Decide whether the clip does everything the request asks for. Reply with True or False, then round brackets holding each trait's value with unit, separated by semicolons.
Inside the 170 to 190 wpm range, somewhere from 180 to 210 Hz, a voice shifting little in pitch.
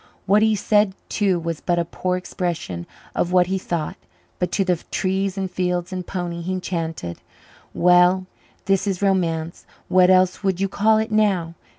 True (175 wpm; 185 Hz; 2.0 semitones)